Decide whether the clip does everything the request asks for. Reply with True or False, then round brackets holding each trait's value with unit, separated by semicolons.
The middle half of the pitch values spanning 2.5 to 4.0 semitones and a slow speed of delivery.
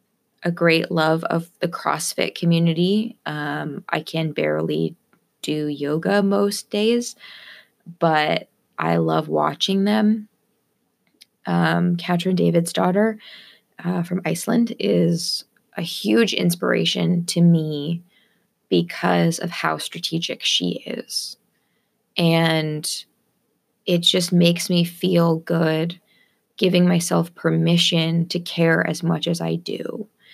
True (3.3 semitones; 110 wpm)